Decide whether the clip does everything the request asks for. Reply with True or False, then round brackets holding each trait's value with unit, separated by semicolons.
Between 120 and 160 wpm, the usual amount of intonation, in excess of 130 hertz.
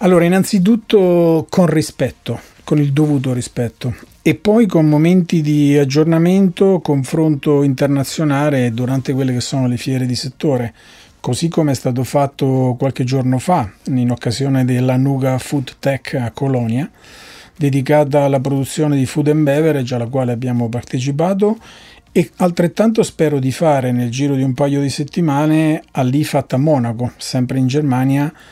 True (145 wpm; 3.3 semitones; 140 Hz)